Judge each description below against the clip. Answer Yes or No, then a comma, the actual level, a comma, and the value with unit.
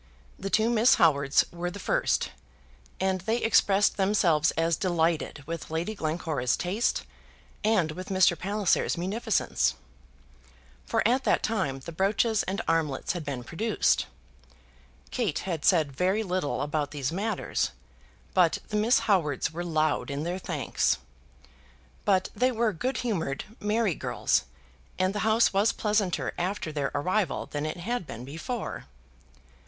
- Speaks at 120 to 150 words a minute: Yes, average, 140 wpm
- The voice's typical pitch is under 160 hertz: No, medium, 185 Hz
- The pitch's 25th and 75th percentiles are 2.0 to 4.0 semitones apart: No, average, 5.1 semitones